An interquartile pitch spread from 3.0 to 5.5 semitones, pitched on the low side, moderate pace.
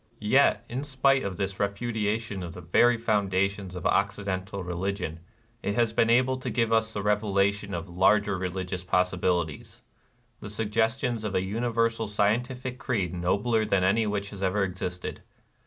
Yes: average, 3.3 semitones; low, 100 Hz; average, 155 wpm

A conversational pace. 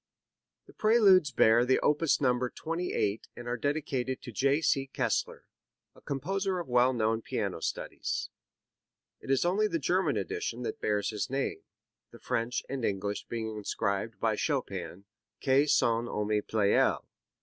Yes: average, 150 wpm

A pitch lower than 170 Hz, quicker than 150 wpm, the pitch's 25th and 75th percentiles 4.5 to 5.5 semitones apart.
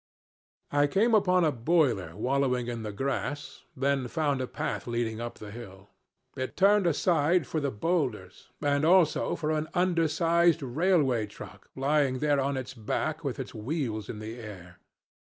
Yes: medium, 140 Hz; average, 160 wpm; average, 5.2 semitones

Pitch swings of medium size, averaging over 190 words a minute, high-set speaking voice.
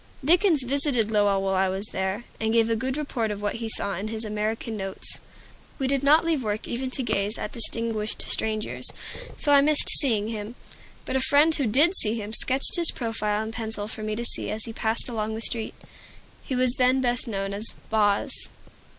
Yes: average, 3.5 semitones; average, 200 wpm; high, 225 Hz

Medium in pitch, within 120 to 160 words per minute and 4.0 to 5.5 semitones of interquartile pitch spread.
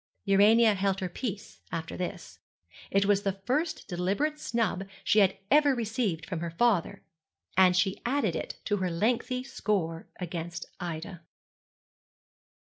No: high, 195 Hz; slow, 135 wpm; average, 4.6 semitones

